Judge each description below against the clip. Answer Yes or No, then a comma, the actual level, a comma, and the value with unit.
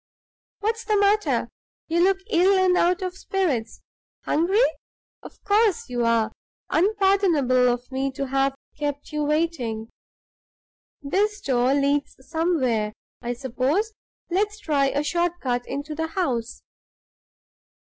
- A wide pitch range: Yes, wide, 6.6 semitones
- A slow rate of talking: Yes, slow, 125 wpm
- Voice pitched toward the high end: Yes, very high, 300 Hz